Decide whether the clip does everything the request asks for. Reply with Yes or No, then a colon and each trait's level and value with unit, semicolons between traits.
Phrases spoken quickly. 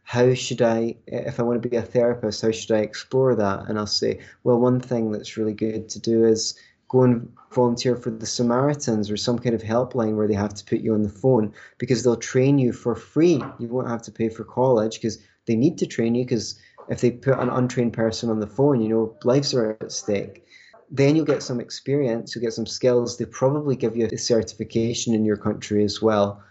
Yes: fast, 230 wpm